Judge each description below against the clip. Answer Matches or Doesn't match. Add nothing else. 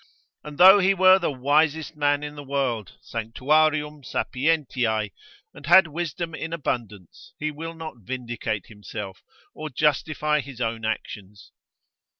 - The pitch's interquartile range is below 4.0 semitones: Doesn't match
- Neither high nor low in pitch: Matches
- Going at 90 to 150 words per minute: Matches